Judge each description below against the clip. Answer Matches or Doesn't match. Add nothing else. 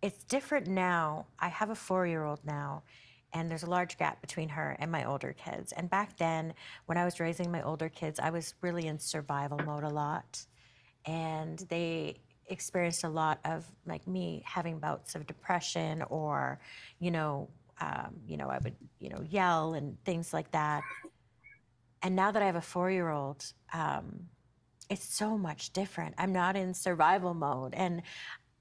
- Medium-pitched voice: Matches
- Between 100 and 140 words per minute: Doesn't match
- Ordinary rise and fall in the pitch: Matches